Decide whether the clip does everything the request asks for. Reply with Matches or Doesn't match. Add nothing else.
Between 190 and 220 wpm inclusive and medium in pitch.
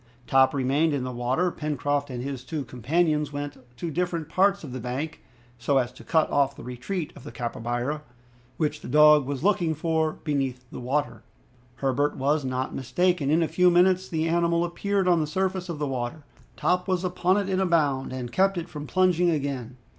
Matches